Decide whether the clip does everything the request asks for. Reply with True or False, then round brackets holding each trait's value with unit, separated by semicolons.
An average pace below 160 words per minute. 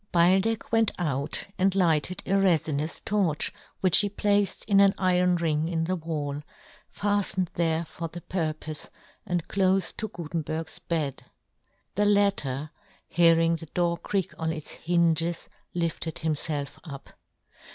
True (140 wpm)